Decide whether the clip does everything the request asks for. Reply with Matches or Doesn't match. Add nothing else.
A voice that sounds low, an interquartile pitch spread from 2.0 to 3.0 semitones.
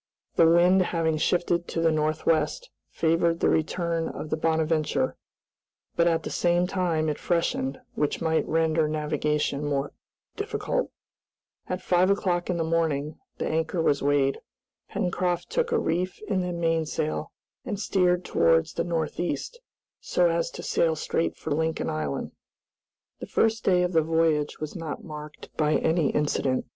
Doesn't match